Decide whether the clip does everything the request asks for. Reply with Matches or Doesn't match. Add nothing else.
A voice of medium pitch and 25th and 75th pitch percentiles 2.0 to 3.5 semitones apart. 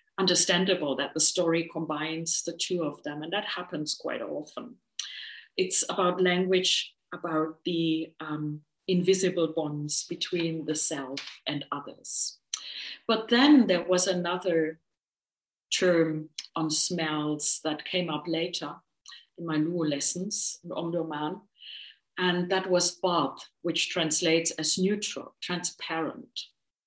Matches